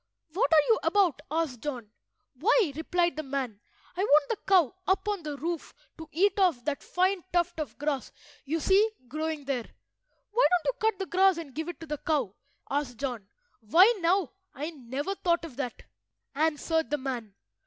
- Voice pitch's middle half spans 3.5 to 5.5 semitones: Yes, average, 4.5 semitones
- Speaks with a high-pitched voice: Yes, very high, 320 Hz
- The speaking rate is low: No, average, 185 wpm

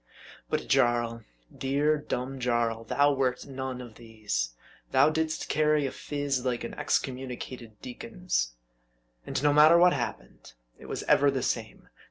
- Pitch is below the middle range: Yes, low, 130 Hz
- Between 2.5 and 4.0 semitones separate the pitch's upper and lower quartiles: Yes, average, 3.4 semitones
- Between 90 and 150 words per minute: Yes, average, 145 wpm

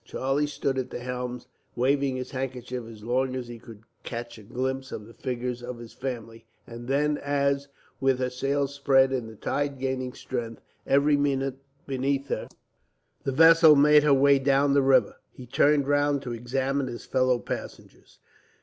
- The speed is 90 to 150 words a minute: No, average, 175 wpm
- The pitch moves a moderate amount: No, narrow, 2.2 semitones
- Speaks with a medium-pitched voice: No, low, 130 Hz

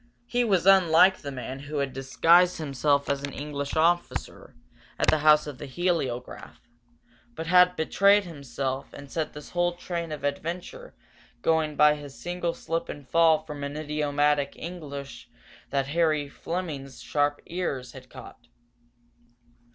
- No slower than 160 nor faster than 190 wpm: No, average, 145 wpm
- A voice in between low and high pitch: Yes, medium, 150 Hz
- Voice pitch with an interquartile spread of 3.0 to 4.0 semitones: Yes, average, 3.4 semitones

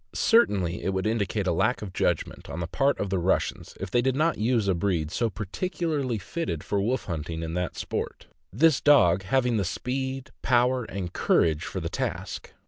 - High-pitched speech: No, low, 105 Hz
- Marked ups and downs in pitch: Yes, wide, 6.4 semitones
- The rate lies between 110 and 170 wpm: No, average, 200 wpm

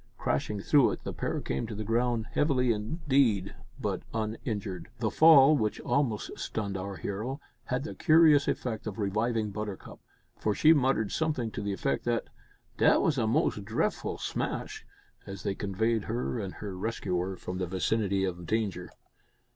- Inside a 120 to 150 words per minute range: No, average, 165 wpm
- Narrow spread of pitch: No, average, 4.3 semitones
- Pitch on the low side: Yes, low, 110 Hz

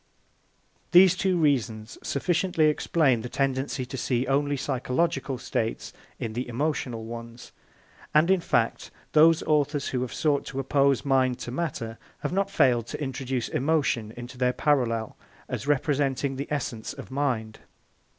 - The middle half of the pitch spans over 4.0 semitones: No, average, 3.5 semitones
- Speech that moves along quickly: No, average, 145 wpm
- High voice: No, low, 135 Hz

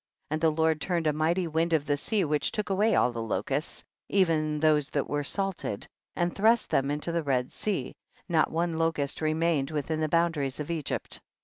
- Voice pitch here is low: No, medium, 155 Hz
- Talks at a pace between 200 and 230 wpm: Yes, fast, 205 wpm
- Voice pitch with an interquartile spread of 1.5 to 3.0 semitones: Yes, narrow, 2.5 semitones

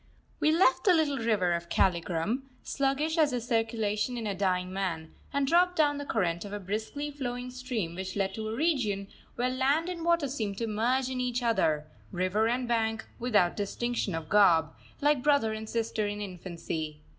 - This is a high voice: Yes, high, 225 Hz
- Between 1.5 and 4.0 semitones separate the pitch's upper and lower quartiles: No, wide, 5.6 semitones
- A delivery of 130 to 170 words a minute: No, average, 185 wpm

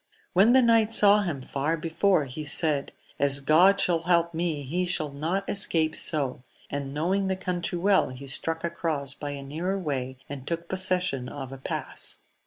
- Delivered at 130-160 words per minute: No, average, 185 wpm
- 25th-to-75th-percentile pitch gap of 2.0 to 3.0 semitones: No, average, 4.6 semitones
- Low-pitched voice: No, medium, 165 Hz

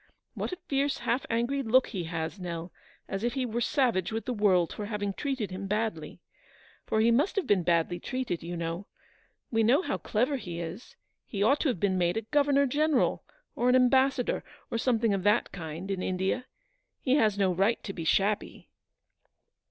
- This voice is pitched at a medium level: No, high, 215 Hz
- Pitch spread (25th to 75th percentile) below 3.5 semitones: No, wide, 5.5 semitones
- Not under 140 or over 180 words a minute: No, average, 190 wpm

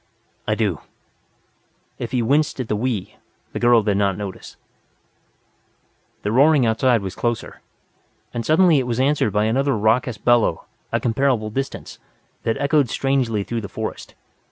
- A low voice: Yes, low, 120 Hz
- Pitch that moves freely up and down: No, average, 3.8 semitones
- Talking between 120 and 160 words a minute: Yes, average, 150 wpm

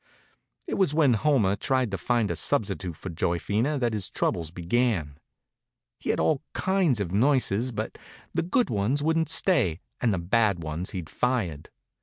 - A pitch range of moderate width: No, wide, 7.1 semitones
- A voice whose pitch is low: Yes, low, 110 Hz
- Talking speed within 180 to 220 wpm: No, average, 165 wpm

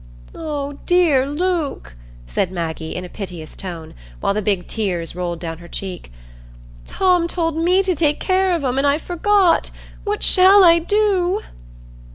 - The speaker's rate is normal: Yes, average, 160 wpm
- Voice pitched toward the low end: No, very high, 295 Hz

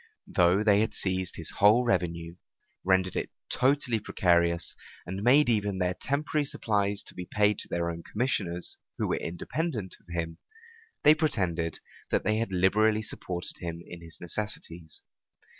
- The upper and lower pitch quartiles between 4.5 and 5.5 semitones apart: No, average, 4.0 semitones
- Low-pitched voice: Yes, very low, 95 Hz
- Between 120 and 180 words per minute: Yes, average, 150 wpm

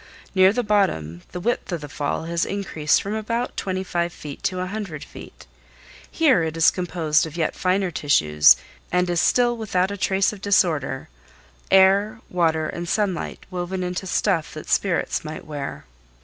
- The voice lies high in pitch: No, medium, 180 Hz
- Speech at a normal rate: Yes, average, 165 wpm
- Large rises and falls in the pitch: No, average, 4.1 semitones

